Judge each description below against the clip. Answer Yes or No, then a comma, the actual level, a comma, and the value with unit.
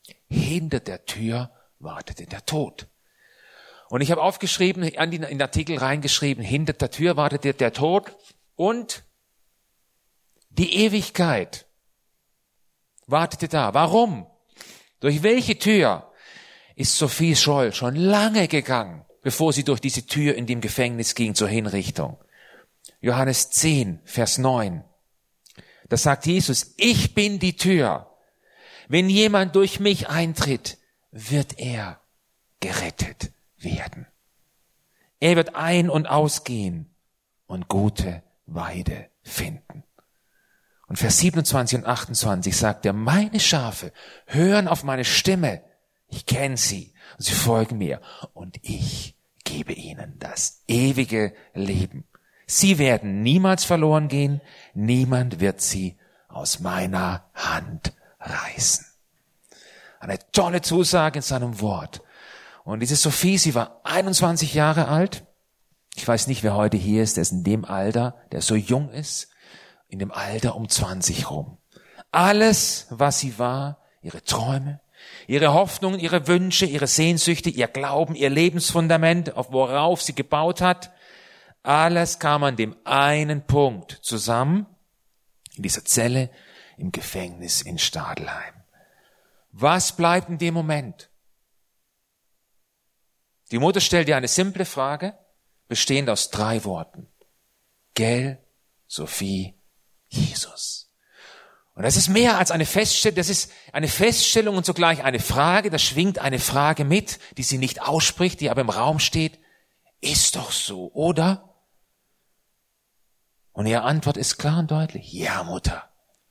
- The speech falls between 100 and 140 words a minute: Yes, slow, 125 wpm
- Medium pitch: Yes, medium, 145 Hz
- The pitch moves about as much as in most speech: No, wide, 6.3 semitones